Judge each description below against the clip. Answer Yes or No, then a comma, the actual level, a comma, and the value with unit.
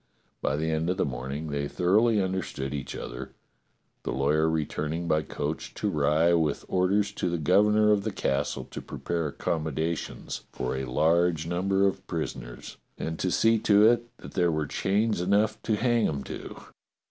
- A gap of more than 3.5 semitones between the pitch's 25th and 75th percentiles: Yes, average, 4.8 semitones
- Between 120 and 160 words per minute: No, average, 175 wpm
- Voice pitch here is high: No, very low, 85 Hz